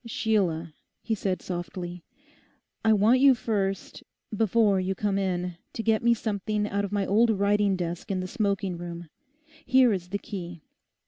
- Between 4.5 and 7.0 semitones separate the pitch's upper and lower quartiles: No, average, 3.2 semitones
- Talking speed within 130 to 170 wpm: Yes, average, 160 wpm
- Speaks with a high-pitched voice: Yes, high, 200 Hz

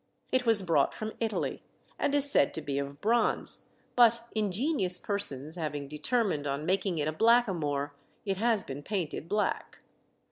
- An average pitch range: No, wide, 7.4 semitones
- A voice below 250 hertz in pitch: Yes, high, 190 Hz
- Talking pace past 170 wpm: No, average, 155 wpm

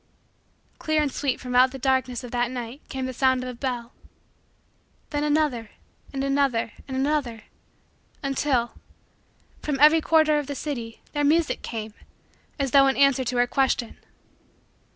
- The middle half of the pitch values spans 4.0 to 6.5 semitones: No, average, 2.8 semitones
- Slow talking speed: No, average, 155 wpm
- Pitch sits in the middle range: No, very high, 265 Hz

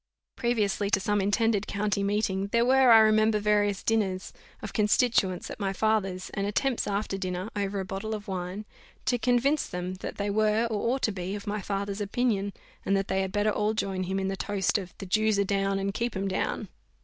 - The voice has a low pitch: No, high, 205 Hz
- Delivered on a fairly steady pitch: Yes, narrow, 1.9 semitones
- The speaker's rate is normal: No, fast, 210 wpm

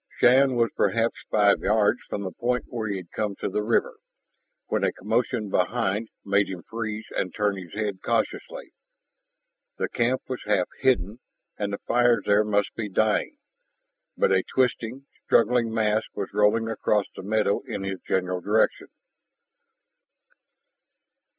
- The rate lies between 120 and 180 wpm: Yes, average, 150 wpm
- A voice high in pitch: No, low, 110 Hz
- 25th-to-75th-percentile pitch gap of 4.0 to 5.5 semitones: No, average, 2.8 semitones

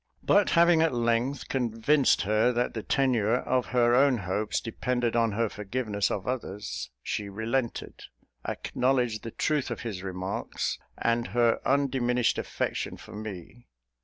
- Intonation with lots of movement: No, average, 3.1 semitones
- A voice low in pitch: Yes, low, 120 Hz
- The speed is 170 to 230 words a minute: No, average, 140 wpm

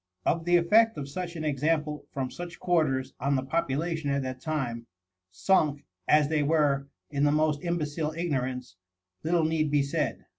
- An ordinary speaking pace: Yes, average, 170 wpm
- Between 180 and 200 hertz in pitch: No, medium, 150 Hz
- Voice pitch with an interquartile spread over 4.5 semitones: No, average, 3.0 semitones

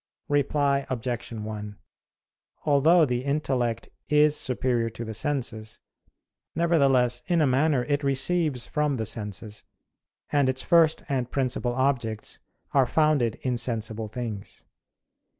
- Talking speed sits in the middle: No, slow, 120 wpm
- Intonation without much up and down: No, average, 4.0 semitones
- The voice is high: No, low, 130 Hz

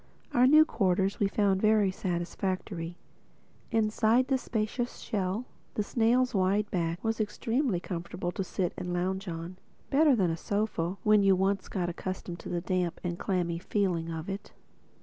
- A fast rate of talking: No, average, 155 wpm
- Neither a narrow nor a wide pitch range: Yes, average, 3.4 semitones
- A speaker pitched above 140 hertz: Yes, high, 190 Hz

